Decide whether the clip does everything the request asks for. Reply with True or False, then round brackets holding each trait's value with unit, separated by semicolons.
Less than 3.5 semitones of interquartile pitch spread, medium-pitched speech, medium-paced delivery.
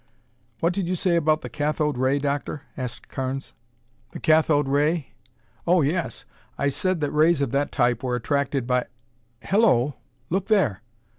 False (3.9 semitones; 145 Hz; 155 wpm)